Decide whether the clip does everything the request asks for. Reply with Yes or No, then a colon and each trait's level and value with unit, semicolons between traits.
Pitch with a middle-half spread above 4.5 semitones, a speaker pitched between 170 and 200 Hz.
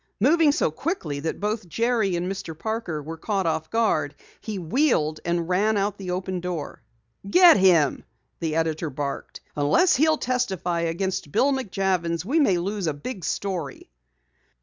Yes: average, 5.3 semitones; medium, 185 Hz